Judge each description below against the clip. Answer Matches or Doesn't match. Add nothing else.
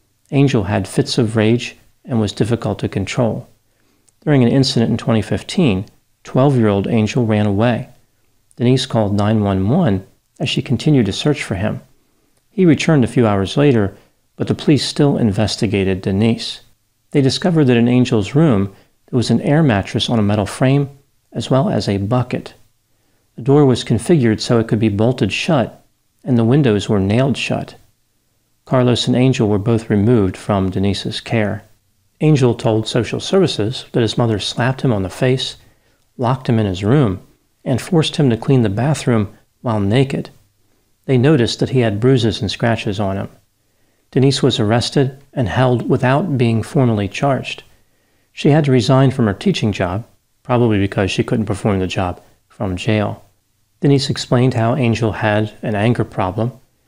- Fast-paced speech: Doesn't match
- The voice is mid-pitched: Doesn't match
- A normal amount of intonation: Matches